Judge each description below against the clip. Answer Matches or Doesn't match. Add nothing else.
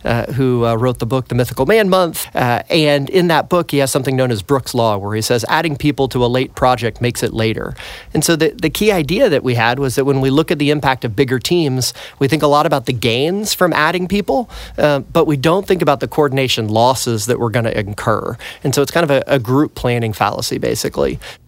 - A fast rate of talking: Matches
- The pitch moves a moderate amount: Matches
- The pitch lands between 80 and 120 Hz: Doesn't match